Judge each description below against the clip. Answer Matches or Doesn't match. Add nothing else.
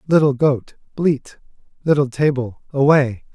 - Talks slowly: Matches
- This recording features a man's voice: Matches